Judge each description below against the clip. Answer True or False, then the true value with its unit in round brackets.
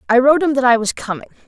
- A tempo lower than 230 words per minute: False (285 wpm)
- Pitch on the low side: False (255 Hz)